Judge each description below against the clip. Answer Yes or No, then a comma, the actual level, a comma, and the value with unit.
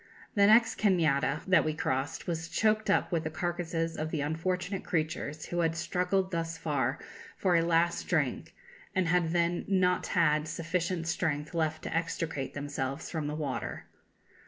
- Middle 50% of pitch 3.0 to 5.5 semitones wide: No, narrow, 2.6 semitones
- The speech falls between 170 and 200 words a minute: No, average, 160 wpm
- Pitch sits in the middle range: Yes, medium, 165 Hz